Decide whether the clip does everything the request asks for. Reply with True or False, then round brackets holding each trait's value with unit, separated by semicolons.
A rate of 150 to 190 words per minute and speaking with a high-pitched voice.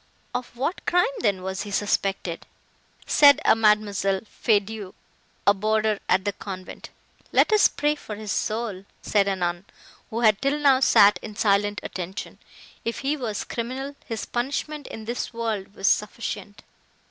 True (155 wpm; 215 Hz)